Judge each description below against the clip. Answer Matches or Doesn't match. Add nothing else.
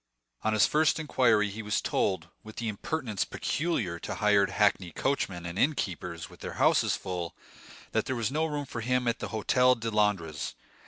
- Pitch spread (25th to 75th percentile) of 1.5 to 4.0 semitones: Doesn't match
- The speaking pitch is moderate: Doesn't match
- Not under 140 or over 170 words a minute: Doesn't match